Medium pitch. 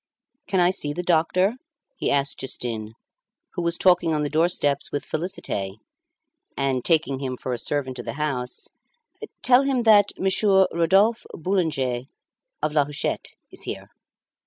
Yes: medium, 155 Hz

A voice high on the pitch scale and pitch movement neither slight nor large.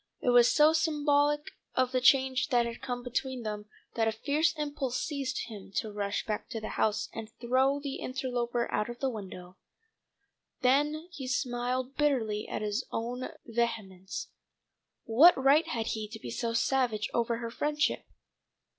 Yes: high, 245 Hz; average, 3.5 semitones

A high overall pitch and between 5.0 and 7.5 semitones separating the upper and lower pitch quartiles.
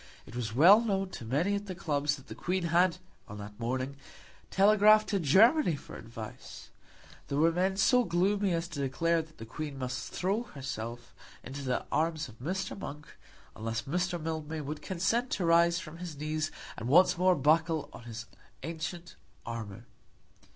No: medium, 160 Hz; wide, 5.5 semitones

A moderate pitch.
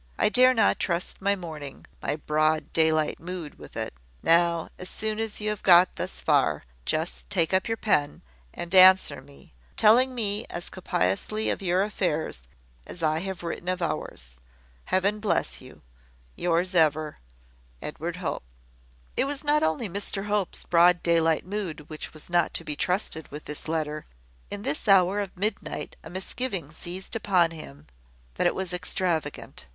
Yes: medium, 175 Hz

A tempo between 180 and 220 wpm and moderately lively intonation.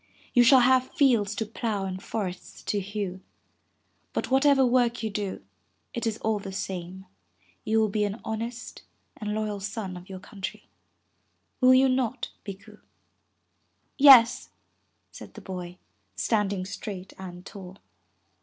No: average, 145 wpm; average, 3.7 semitones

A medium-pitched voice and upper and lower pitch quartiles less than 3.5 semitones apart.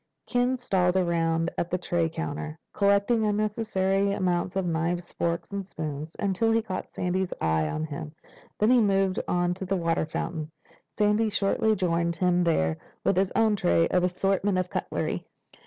Yes: medium, 180 Hz; average, 3.1 semitones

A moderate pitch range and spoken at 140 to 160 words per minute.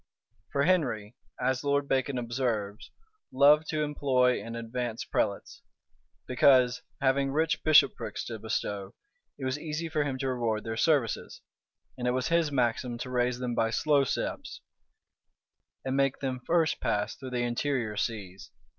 Yes: average, 3.3 semitones; average, 150 wpm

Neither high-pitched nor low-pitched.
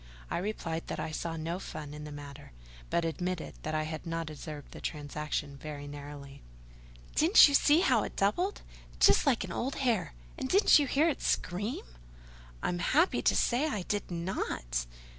Yes: medium, 170 Hz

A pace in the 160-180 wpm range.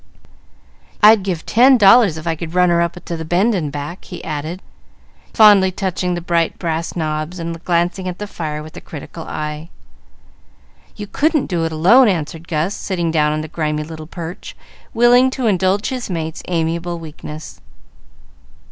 Yes: average, 170 wpm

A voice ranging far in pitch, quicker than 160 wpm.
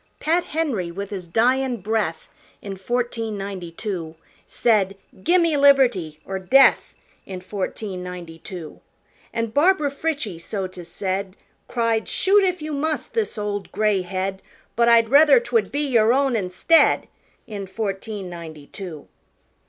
No: wide, 6.2 semitones; average, 140 wpm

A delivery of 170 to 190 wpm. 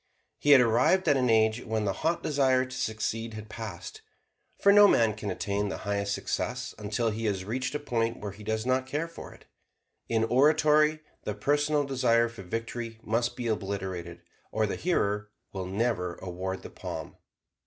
Yes: average, 180 wpm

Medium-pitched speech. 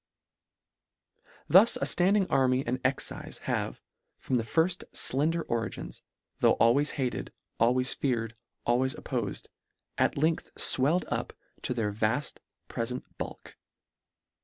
No: low, 130 Hz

